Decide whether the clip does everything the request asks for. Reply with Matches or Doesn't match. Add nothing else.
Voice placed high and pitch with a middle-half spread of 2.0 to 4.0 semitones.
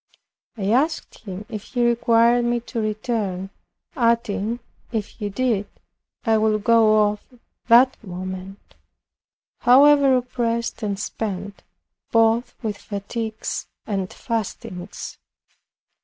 Matches